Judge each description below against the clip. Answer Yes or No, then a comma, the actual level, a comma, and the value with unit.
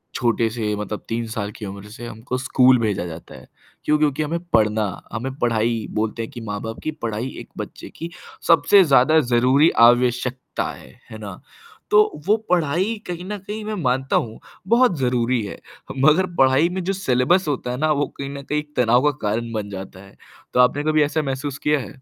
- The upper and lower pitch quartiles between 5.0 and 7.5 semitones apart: Yes, average, 5.3 semitones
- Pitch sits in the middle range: No, low, 125 Hz